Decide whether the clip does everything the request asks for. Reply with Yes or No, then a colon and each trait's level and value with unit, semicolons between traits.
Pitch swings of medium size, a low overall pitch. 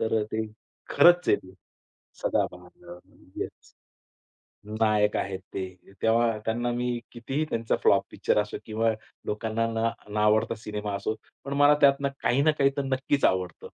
Yes: average, 4.1 semitones; low, 115 Hz